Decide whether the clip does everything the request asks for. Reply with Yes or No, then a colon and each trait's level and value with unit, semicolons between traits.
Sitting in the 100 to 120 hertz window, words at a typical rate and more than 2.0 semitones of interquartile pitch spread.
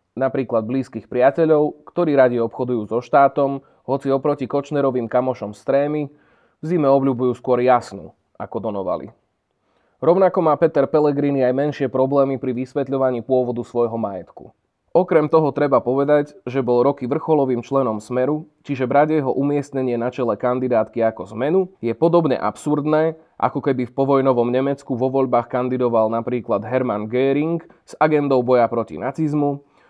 No: low, 135 Hz; average, 140 wpm; average, 2.9 semitones